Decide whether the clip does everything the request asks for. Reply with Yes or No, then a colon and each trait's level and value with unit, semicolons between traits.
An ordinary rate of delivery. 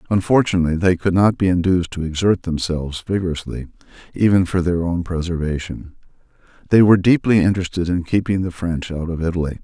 Yes: average, 160 wpm